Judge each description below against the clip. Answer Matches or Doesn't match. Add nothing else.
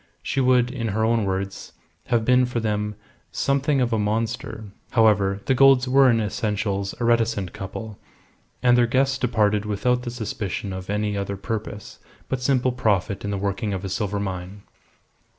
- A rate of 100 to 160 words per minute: Doesn't match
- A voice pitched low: Matches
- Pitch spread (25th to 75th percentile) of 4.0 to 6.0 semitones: Doesn't match